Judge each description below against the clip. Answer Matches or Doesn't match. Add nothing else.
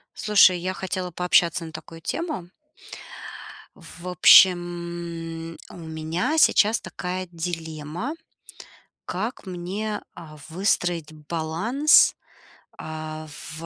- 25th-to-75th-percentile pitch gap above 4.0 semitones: Doesn't match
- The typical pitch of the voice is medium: Matches